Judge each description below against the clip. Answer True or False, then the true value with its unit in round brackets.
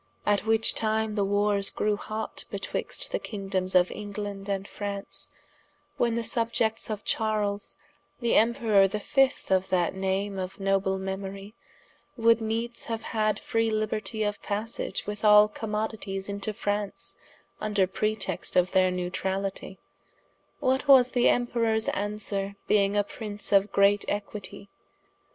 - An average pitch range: False (2.0 semitones)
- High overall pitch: True (205 Hz)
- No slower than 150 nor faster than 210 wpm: False (135 wpm)